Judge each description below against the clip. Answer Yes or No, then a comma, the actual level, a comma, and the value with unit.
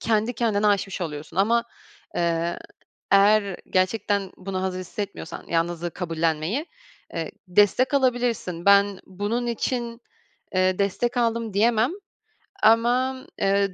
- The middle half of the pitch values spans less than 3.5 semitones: No, average, 4.0 semitones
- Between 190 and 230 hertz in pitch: Yes, high, 200 Hz